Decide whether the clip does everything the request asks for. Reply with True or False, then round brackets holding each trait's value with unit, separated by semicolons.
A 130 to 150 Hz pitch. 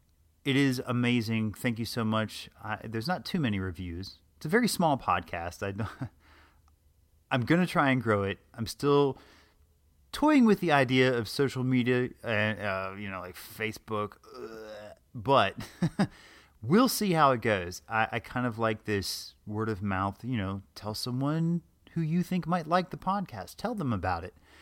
False (110 Hz)